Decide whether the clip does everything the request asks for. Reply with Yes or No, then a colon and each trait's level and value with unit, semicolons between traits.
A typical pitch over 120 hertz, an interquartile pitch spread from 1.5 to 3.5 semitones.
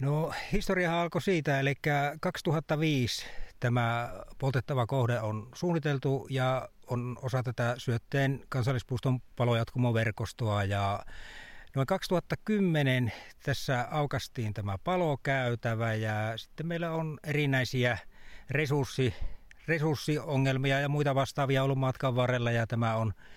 No: low, 130 Hz; average, 3.9 semitones